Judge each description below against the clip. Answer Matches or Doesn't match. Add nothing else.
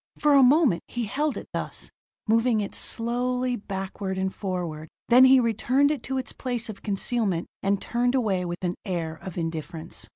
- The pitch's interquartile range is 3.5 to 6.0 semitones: Matches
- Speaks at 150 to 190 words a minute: Matches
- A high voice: Matches